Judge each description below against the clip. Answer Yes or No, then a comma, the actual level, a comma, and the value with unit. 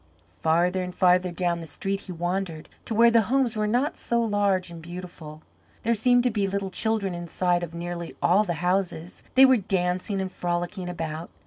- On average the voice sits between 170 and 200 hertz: Yes, medium, 185 Hz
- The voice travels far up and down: No, average, 3.2 semitones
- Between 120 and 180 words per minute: No, average, 190 wpm